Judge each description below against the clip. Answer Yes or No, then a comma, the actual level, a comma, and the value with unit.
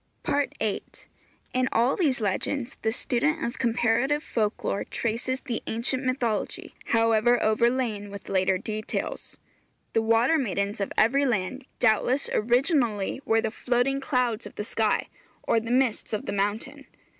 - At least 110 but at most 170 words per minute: Yes, average, 145 wpm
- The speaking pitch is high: Yes, high, 235 Hz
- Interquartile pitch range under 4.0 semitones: Yes, average, 3.1 semitones